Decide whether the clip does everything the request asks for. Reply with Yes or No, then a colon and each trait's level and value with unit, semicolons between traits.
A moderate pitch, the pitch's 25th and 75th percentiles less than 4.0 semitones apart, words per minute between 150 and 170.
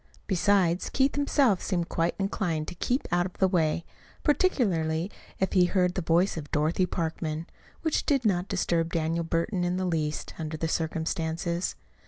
Yes: medium, 175 Hz; average, 2.9 semitones; average, 165 wpm